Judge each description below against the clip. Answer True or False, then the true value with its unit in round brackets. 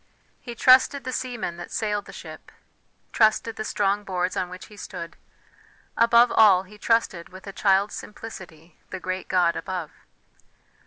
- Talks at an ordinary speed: True (155 wpm)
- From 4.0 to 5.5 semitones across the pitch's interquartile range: False (3.6 semitones)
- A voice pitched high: True (200 Hz)